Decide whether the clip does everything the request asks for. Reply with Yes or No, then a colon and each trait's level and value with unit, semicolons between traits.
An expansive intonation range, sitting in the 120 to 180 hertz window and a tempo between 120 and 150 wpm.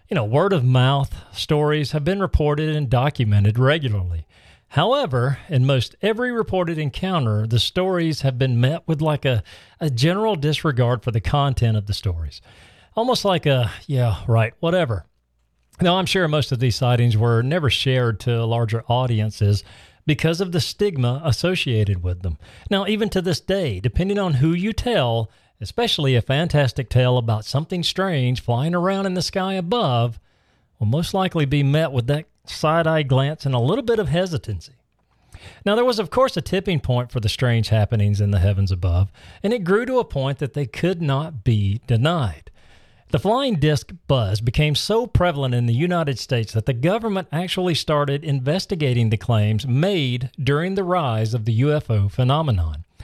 No: wide, 6.7 semitones; low, 135 Hz; average, 175 wpm